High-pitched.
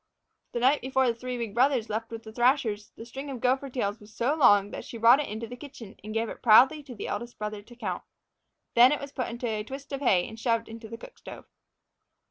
Yes: high, 235 Hz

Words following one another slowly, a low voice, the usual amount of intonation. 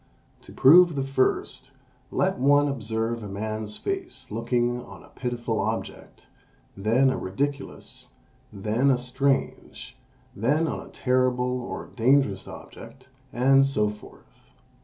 Yes: slow, 125 wpm; low, 125 Hz; average, 3.5 semitones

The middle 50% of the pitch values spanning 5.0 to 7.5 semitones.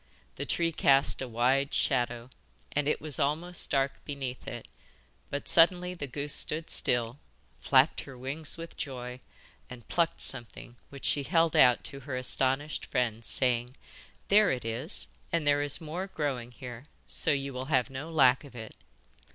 No: average, 3.5 semitones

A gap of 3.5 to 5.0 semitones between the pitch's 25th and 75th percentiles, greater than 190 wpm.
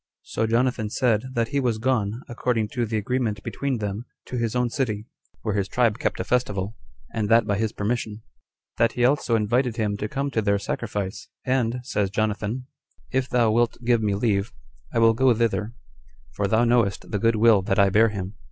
No: average, 2.7 semitones; average, 200 wpm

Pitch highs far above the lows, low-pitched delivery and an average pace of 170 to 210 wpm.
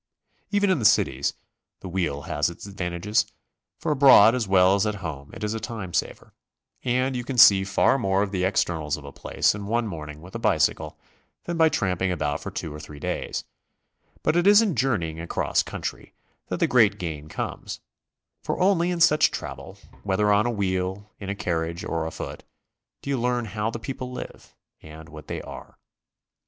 Yes: wide, 6.3 semitones; low, 100 Hz; average, 195 wpm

